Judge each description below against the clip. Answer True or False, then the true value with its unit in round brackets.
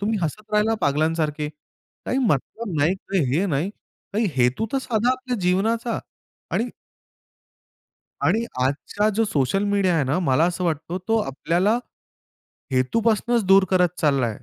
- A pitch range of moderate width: False (6.6 semitones)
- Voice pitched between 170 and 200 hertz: True (190 Hz)